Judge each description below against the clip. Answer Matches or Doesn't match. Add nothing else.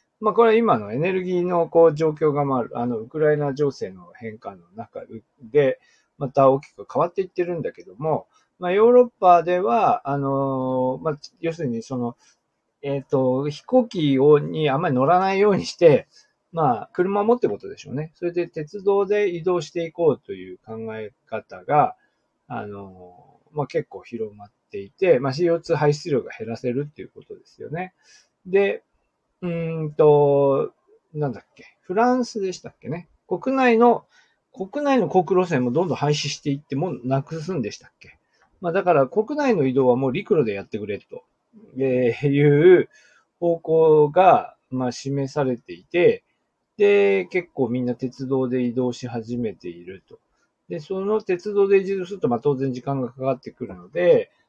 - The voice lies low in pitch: Doesn't match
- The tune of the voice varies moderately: Doesn't match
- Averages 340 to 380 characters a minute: Doesn't match